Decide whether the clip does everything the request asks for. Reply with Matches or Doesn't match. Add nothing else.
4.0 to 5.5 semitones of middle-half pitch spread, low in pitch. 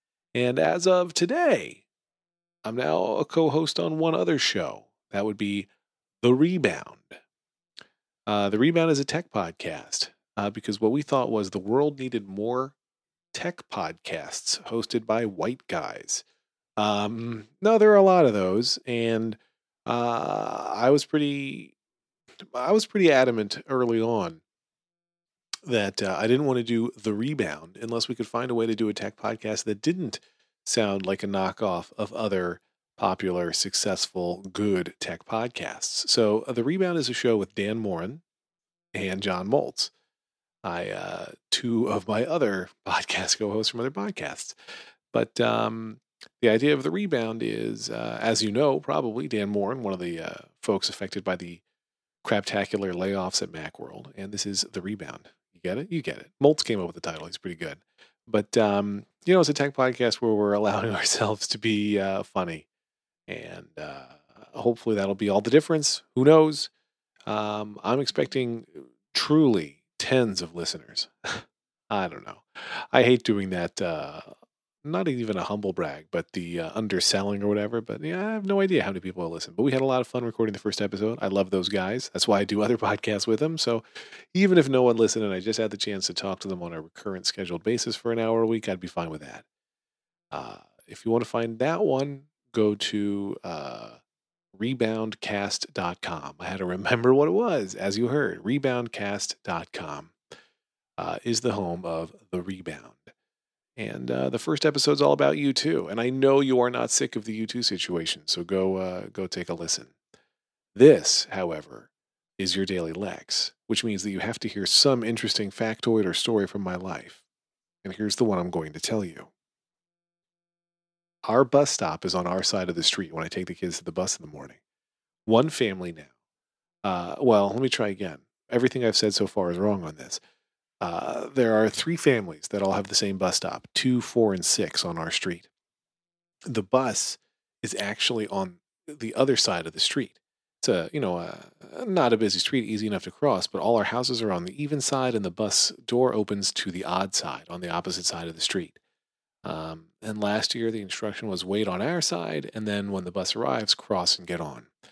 Matches